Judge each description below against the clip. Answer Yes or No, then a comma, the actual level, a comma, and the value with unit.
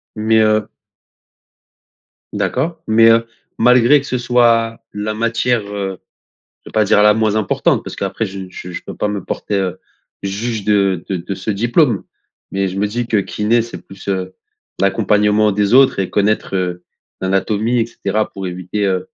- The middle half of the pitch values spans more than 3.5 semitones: No, average, 2.8 semitones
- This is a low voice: Yes, low, 105 Hz